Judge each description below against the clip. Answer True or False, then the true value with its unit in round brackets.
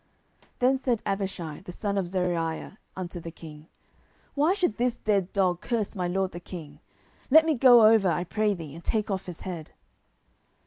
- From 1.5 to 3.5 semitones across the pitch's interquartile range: False (4.1 semitones)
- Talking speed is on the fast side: False (185 wpm)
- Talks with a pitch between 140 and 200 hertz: True (190 Hz)